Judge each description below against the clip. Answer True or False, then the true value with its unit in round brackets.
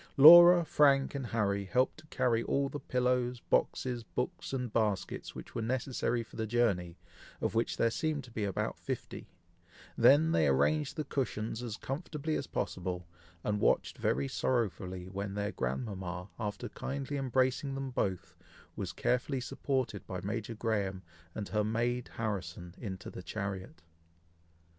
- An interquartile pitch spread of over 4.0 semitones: True (5.0 semitones)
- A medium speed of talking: True (150 wpm)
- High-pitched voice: False (115 Hz)